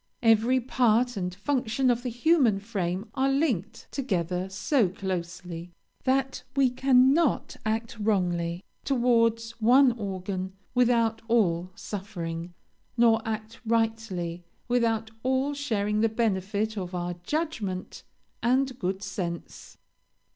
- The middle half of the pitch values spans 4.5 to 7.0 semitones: Yes, average, 4.8 semitones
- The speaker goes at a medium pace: No, slow, 110 wpm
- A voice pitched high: Yes, high, 225 Hz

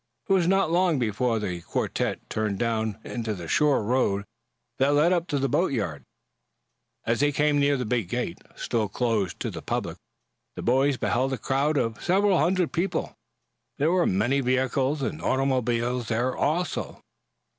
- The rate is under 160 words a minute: No, average, 165 wpm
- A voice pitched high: No, low, 130 Hz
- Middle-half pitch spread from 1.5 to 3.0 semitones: No, average, 4.8 semitones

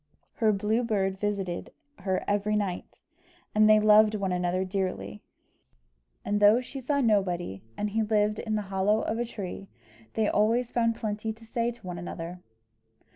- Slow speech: No, average, 165 wpm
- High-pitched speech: Yes, high, 210 Hz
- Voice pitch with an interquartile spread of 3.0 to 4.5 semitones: No, narrow, 2.4 semitones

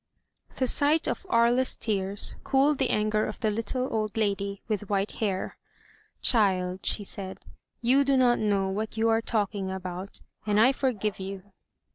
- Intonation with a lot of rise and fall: No, average, 3.5 semitones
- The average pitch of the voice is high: Yes, high, 215 Hz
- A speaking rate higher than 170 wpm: No, average, 160 wpm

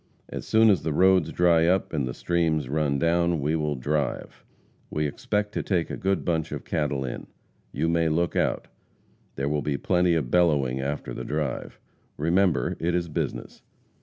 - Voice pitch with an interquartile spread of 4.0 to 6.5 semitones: No, average, 3.1 semitones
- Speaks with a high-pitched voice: No, very low, 80 Hz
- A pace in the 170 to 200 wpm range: Yes, average, 180 wpm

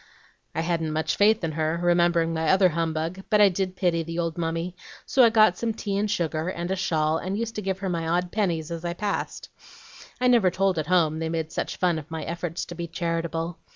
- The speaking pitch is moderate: Yes, medium, 170 Hz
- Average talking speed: No, fast, 230 wpm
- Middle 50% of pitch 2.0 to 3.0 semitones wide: Yes, average, 2.7 semitones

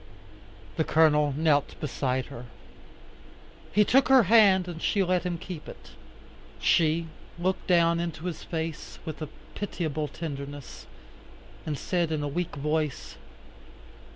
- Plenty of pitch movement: No, average, 3.1 semitones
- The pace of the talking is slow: Yes, slow, 130 wpm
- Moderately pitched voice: Yes, medium, 160 Hz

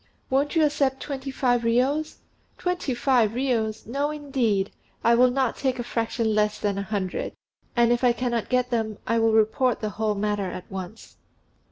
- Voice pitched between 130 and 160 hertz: No, high, 235 Hz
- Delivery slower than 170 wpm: No, average, 180 wpm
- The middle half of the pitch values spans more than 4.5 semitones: No, average, 3.5 semitones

